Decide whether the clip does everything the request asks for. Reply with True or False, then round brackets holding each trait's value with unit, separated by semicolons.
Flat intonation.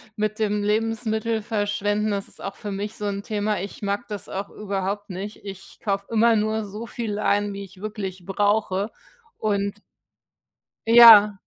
True (1.3 semitones)